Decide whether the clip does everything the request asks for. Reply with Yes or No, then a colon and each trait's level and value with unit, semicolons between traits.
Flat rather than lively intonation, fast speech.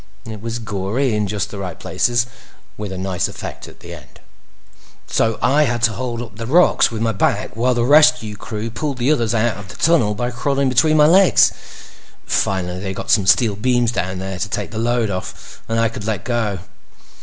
No: average, 3.3 semitones; fast, 210 wpm